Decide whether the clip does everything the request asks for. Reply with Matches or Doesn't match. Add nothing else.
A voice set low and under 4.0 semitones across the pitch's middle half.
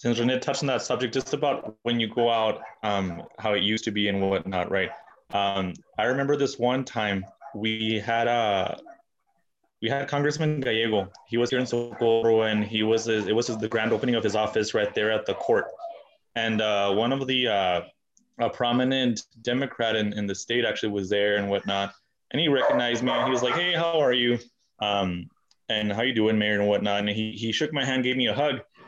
Matches